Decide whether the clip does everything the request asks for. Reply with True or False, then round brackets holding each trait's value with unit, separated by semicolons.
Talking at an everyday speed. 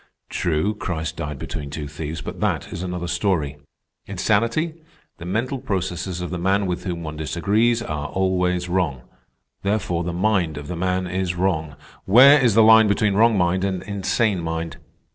True (170 wpm)